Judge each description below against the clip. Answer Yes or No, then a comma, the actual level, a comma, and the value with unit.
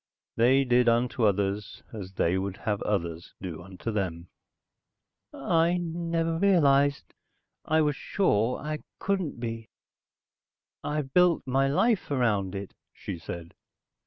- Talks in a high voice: No, low, 125 Hz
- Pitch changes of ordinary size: No, wide, 7.7 semitones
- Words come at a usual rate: No, slow, 125 wpm